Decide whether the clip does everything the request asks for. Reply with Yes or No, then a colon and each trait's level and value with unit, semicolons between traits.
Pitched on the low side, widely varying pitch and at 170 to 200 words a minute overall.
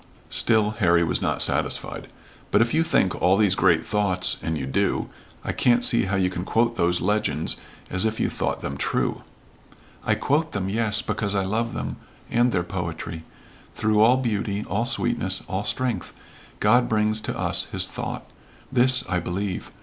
No: low, 105 Hz; average, 4.0 semitones; average, 175 wpm